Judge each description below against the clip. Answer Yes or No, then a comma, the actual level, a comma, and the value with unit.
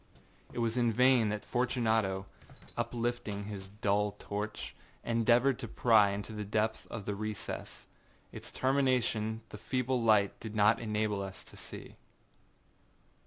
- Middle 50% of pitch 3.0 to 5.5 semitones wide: No, narrow, 2.5 semitones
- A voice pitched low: Yes, low, 110 Hz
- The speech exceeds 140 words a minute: No, slow, 135 wpm